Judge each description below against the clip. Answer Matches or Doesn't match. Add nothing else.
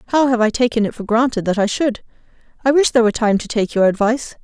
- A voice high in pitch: Matches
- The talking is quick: Matches